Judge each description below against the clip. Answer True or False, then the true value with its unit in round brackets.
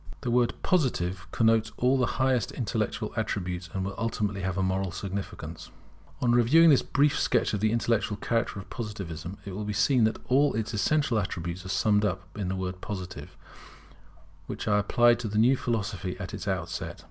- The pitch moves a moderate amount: True (3.9 semitones)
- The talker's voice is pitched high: False (105 Hz)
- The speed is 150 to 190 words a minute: True (185 wpm)